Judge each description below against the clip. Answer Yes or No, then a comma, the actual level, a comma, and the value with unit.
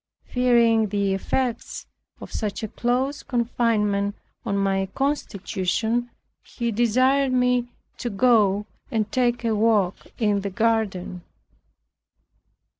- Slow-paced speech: Yes, slow, 110 wpm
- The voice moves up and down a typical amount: Yes, average, 3.2 semitones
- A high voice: Yes, high, 225 Hz